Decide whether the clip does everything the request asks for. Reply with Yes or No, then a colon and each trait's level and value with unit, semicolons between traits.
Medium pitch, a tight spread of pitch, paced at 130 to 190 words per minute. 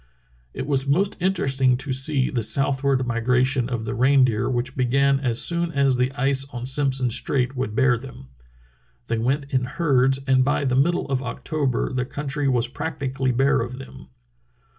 No: low, 130 Hz; narrow, 1.7 semitones; average, 180 wpm